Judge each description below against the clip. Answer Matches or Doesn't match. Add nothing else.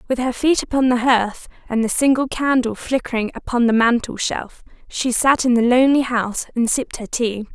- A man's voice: Doesn't match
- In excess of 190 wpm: Matches